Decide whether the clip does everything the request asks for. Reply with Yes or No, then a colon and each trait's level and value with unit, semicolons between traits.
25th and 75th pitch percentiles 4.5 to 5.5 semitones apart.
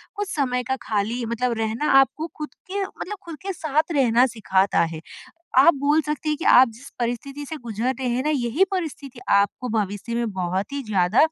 Yes: average, 5.2 semitones